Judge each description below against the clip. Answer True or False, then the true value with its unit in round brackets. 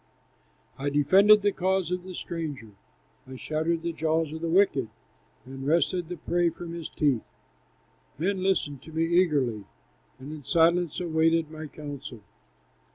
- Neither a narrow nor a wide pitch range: True (3.2 semitones)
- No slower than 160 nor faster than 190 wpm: False (150 wpm)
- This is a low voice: False (160 Hz)